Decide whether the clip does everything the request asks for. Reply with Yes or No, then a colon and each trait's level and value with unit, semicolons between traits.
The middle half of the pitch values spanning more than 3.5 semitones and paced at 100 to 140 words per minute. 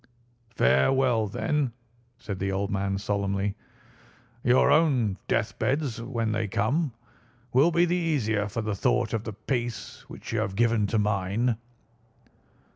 Yes: average, 4.3 semitones; slow, 135 wpm